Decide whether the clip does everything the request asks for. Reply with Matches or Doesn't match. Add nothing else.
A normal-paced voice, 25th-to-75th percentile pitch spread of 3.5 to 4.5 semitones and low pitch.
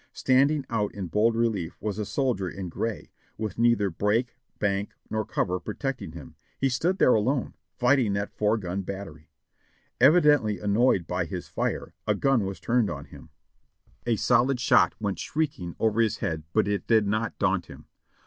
Matches